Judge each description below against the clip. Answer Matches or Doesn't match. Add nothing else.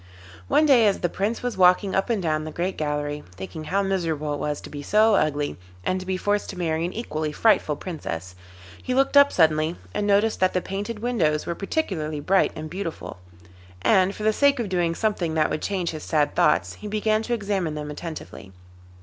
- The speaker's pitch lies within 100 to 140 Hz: Doesn't match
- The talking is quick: Matches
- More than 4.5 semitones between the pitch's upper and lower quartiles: Matches